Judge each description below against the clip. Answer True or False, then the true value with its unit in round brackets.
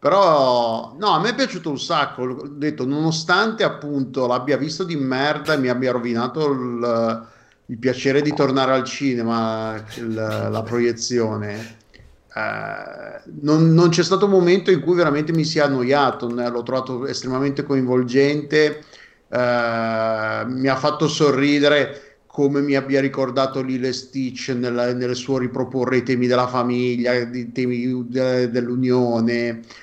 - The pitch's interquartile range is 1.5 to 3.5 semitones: True (3.0 semitones)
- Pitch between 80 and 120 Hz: False (130 Hz)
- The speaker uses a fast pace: False (145 wpm)